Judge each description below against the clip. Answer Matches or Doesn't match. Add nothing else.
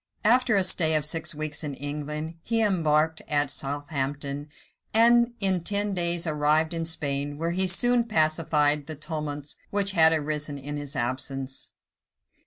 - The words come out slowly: Doesn't match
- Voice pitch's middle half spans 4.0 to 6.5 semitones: Doesn't match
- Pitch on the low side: Doesn't match